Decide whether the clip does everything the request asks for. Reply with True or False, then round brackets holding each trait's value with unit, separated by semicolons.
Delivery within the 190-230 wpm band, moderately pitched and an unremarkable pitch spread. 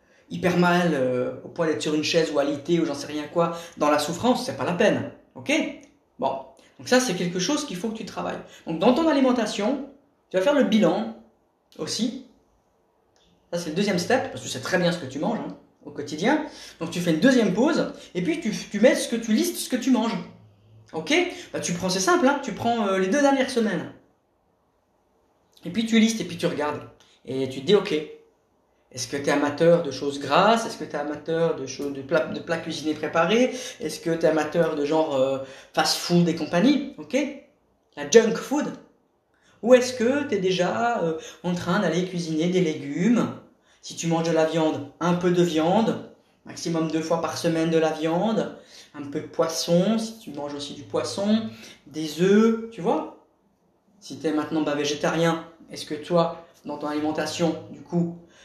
False (210 wpm; 175 Hz; 6.6 semitones)